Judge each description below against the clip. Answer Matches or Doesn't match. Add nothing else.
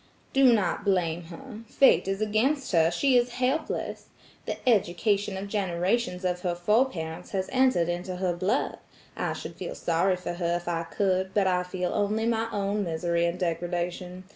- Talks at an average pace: Matches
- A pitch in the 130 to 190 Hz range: Matches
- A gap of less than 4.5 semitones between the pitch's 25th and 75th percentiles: Matches